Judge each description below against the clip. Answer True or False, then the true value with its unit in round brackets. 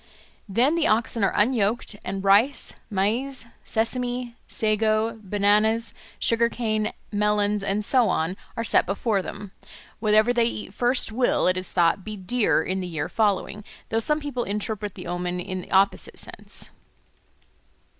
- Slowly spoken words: False (150 wpm)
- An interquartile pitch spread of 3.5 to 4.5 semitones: False (3.0 semitones)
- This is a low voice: False (215 Hz)